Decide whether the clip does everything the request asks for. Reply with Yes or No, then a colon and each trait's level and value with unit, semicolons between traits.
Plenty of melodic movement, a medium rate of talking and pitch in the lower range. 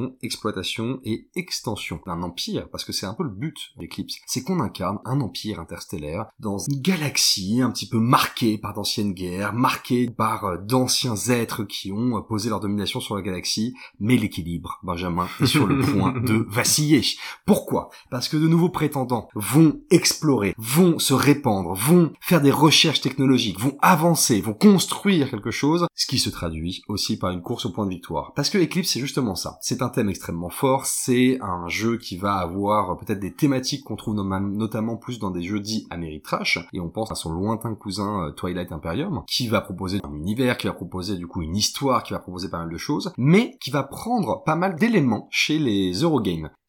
Yes: wide, 6.1 semitones; average, 195 wpm; low, 110 Hz